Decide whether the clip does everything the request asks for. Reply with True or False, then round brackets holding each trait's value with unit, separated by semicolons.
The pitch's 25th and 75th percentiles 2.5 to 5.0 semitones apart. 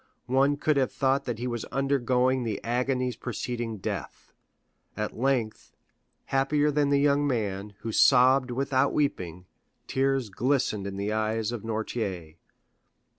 True (3.9 semitones)